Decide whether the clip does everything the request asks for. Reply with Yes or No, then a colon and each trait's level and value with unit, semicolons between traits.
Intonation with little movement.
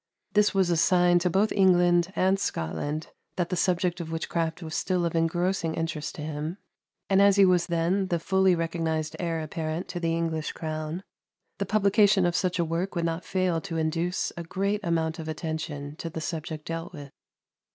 Yes: narrow, 2.3 semitones